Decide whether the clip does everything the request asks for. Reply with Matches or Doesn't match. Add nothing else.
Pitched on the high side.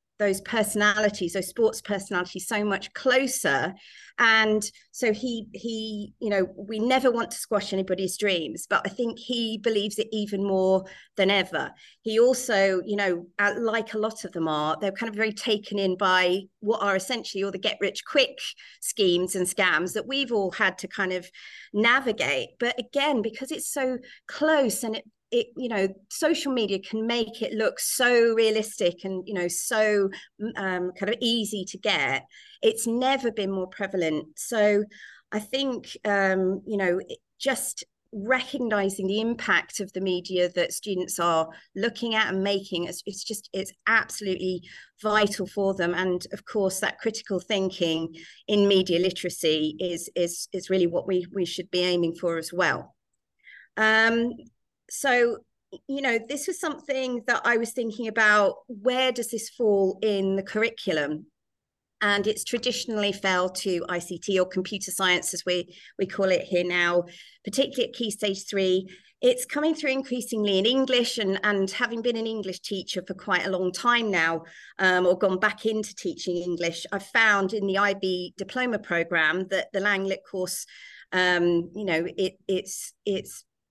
Matches